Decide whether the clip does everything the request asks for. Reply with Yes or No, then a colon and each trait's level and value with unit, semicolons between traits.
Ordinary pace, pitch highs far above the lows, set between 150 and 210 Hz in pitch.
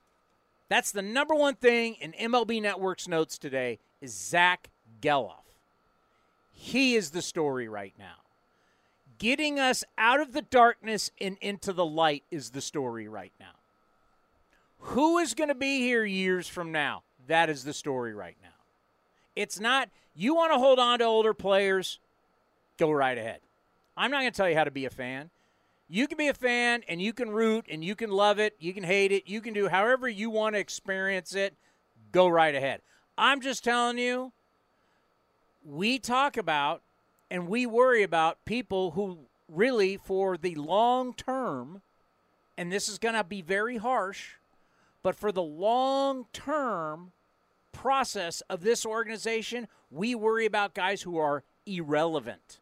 Yes: average, 165 wpm; wide, 8.5 semitones; high, 190 Hz